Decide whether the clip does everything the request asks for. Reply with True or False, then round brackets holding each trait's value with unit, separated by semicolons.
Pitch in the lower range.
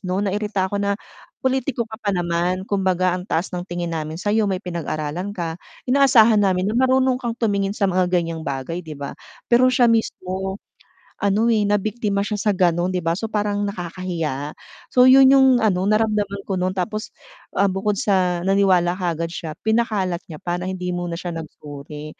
False (190 Hz)